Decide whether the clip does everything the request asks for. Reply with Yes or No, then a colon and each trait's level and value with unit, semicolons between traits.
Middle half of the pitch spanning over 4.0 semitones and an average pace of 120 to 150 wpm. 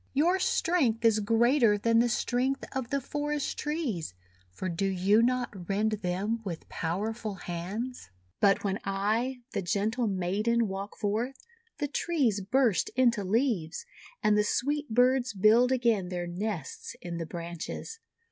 Yes: average, 4.5 semitones; average, 145 wpm